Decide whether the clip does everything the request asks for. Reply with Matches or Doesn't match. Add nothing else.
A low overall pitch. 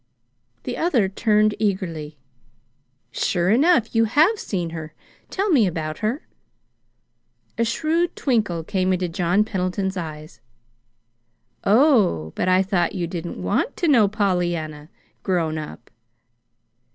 Doesn't match